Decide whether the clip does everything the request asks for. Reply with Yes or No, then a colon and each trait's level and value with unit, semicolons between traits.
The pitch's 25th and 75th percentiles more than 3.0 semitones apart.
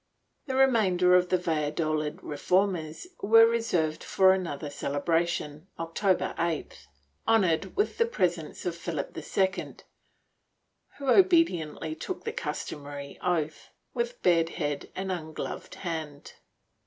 Yes: average, 4.3 semitones